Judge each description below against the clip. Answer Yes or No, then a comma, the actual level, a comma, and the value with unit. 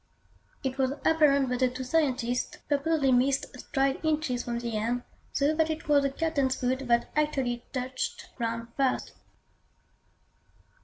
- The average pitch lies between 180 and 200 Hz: No, very high, 265 Hz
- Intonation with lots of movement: No, average, 3.0 semitones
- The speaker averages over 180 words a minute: No, average, 145 wpm